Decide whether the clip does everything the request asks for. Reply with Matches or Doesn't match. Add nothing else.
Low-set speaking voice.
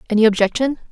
Doesn't match